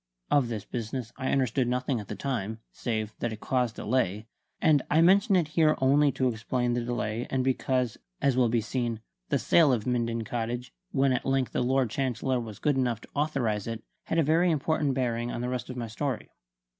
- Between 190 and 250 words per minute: Yes, fast, 205 wpm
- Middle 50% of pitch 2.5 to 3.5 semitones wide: Yes, average, 2.8 semitones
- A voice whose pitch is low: Yes, low, 125 Hz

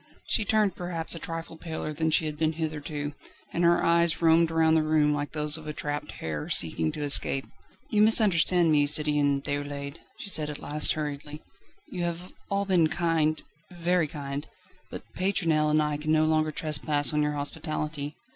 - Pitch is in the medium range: Yes, medium, 155 Hz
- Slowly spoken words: No, average, 180 wpm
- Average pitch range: No, narrow, 2.1 semitones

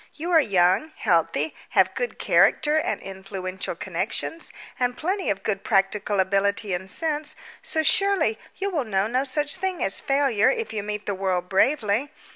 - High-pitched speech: Yes, high, 220 Hz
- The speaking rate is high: No, average, 165 wpm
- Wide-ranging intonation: Yes, wide, 8.1 semitones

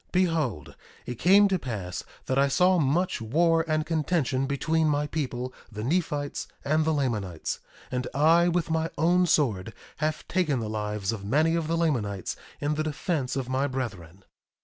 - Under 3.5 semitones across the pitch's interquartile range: No, average, 5.0 semitones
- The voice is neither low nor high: Yes, medium, 145 Hz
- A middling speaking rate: Yes, average, 170 wpm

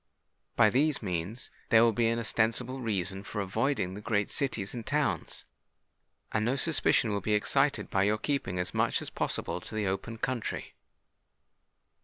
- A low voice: Yes, low, 110 Hz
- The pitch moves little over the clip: No, average, 3.7 semitones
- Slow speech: No, average, 165 wpm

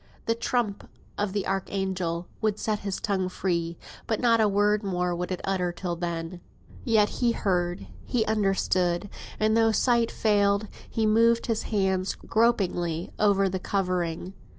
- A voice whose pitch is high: Yes, high, 195 Hz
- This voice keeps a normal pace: Yes, average, 150 wpm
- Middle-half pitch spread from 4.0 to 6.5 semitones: No, average, 3.2 semitones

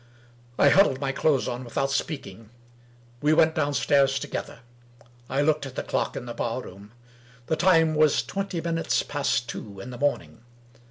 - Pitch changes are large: No, average, 4.3 semitones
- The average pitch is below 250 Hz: Yes, medium, 140 Hz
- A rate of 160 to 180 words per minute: Yes, average, 170 wpm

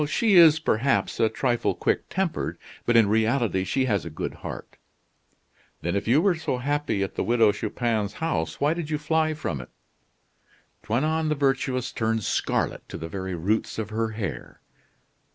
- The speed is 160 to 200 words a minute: Yes, average, 170 wpm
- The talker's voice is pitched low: Yes, low, 120 Hz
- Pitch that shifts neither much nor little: No, wide, 6.2 semitones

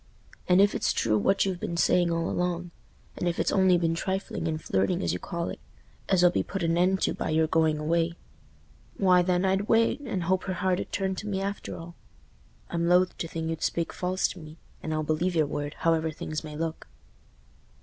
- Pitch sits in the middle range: Yes, medium, 170 Hz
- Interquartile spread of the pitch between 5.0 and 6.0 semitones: No, narrow, 2.5 semitones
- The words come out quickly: Yes, fast, 210 wpm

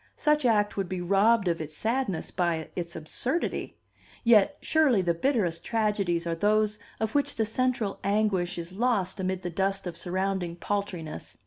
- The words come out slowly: No, average, 160 wpm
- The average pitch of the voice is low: No, high, 195 Hz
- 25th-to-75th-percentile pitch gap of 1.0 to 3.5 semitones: No, average, 4.1 semitones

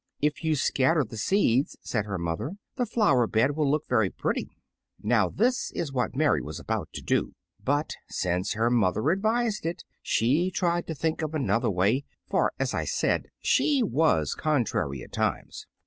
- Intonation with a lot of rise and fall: Yes, wide, 7.0 semitones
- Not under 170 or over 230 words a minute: Yes, average, 175 wpm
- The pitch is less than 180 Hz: Yes, medium, 140 Hz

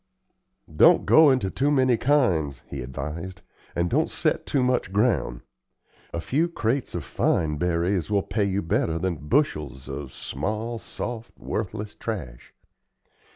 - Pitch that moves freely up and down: Yes, wide, 7.9 semitones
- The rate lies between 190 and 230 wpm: No, average, 140 wpm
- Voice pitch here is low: Yes, very low, 95 Hz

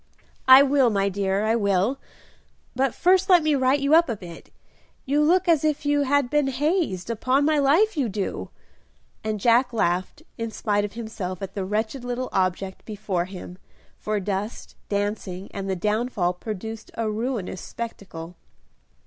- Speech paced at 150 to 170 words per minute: Yes, average, 165 wpm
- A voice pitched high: Yes, high, 225 Hz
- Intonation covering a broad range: Yes, wide, 5.9 semitones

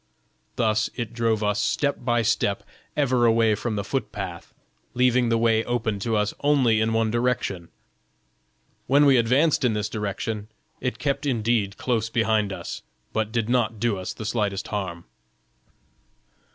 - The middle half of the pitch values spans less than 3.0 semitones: Yes, narrow, 2.5 semitones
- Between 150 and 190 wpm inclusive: Yes, average, 155 wpm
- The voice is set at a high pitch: No, low, 115 Hz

